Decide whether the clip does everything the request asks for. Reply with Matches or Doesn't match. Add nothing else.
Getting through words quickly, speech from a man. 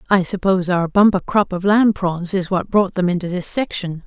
Doesn't match